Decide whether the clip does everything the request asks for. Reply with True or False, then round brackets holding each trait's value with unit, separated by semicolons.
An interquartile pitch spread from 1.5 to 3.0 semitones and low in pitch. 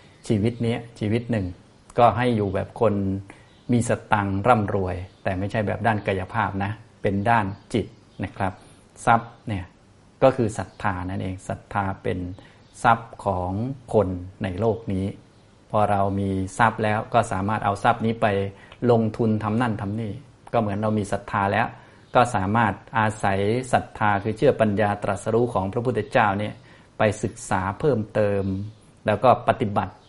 True (2.5 semitones; 105 Hz)